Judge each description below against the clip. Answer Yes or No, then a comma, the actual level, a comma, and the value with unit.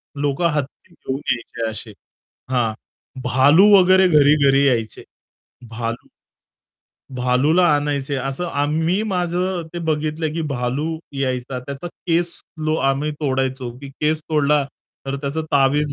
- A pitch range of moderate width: Yes, average, 3.1 semitones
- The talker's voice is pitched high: No, medium, 145 Hz